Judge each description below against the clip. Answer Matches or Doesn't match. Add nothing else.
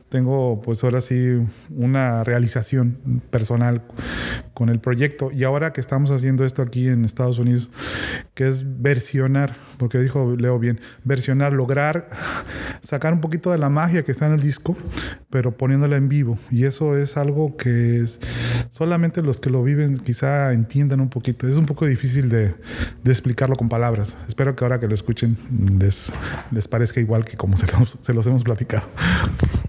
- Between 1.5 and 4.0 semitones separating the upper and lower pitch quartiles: Matches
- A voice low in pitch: Matches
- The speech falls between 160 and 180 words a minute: Matches